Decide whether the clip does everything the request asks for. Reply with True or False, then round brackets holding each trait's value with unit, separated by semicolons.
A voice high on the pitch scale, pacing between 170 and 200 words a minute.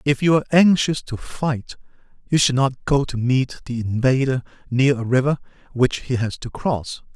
False (130 Hz; 185 wpm)